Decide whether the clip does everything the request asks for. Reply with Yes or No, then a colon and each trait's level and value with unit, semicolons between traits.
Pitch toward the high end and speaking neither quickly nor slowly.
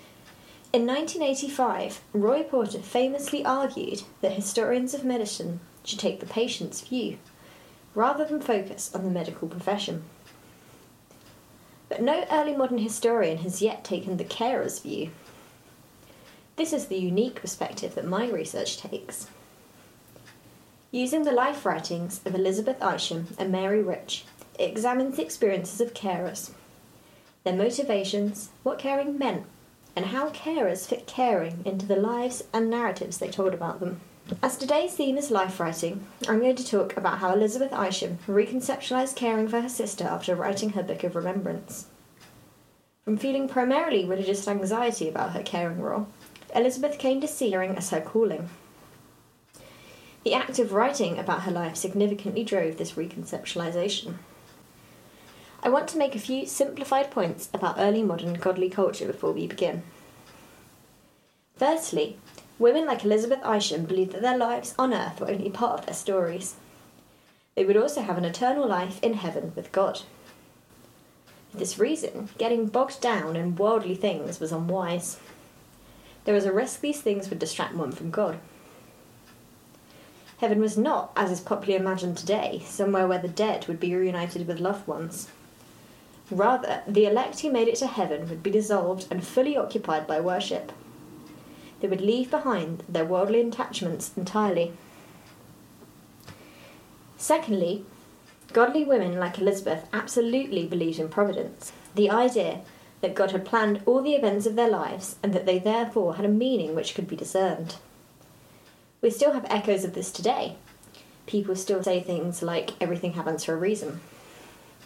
Yes: high, 205 Hz; average, 150 wpm